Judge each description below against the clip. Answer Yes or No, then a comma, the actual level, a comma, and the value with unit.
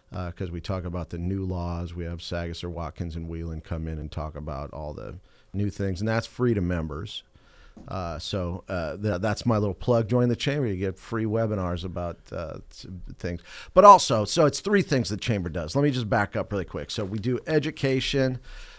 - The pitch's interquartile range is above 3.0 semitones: Yes, average, 4.8 semitones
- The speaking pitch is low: Yes, very low, 95 Hz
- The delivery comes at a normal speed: No, fast, 215 wpm